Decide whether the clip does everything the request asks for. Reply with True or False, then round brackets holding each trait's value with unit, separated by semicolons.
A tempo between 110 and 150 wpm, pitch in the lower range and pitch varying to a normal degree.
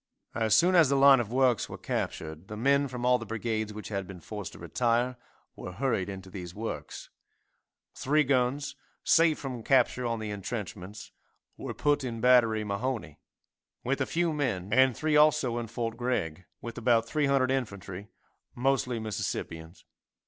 False (165 wpm; 120 Hz; 4.4 semitones)